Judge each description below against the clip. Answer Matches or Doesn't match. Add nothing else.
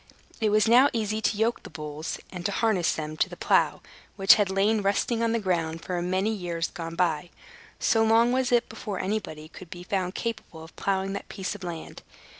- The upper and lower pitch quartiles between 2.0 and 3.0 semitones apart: Doesn't match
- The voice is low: Doesn't match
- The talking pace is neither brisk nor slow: Doesn't match